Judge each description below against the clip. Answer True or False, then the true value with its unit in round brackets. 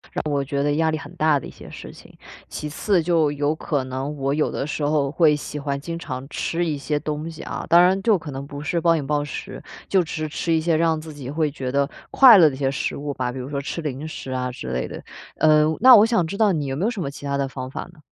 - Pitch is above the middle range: False (150 Hz)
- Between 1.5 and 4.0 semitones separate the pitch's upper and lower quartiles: True (2.9 semitones)